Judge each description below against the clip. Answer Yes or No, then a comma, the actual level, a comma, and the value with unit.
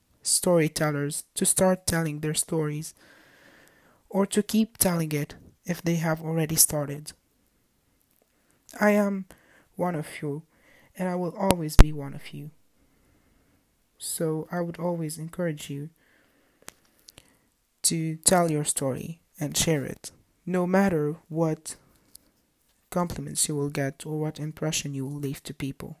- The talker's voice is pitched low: No, medium, 160 Hz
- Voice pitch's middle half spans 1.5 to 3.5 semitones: Yes, average, 2.9 semitones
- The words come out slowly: Yes, slow, 130 wpm